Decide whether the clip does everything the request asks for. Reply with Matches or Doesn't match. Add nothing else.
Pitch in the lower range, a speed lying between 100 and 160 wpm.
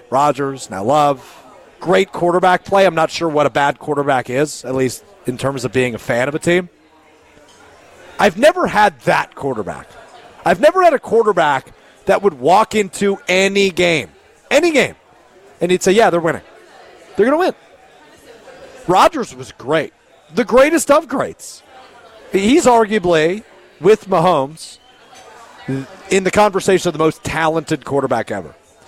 Doesn't match